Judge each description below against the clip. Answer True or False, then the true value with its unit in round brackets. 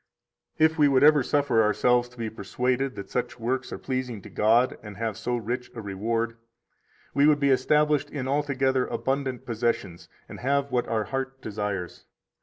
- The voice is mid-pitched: False (125 Hz)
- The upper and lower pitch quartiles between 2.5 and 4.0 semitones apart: True (3.2 semitones)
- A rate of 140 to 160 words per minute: False (180 wpm)